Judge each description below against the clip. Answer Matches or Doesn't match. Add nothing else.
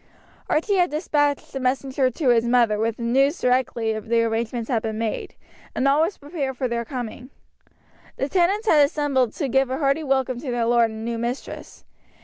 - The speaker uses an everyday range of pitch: Matches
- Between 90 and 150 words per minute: Doesn't match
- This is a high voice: Matches